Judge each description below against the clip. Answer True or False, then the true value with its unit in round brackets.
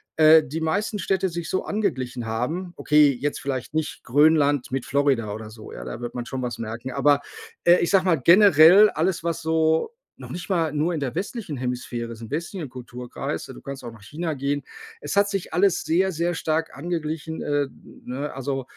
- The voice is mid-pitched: True (150 Hz)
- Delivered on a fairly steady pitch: False (5.0 semitones)